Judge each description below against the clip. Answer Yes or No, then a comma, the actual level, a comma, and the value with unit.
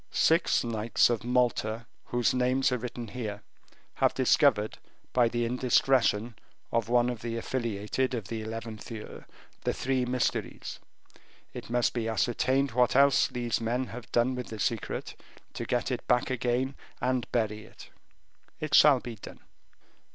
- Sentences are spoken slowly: No, average, 150 wpm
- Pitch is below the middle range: Yes, low, 120 Hz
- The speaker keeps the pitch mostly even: Yes, narrow, 1.9 semitones